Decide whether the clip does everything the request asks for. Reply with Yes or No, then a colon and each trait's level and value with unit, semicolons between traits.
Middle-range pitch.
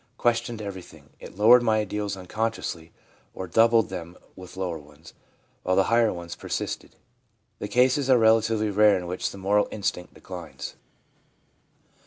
No: low, 105 Hz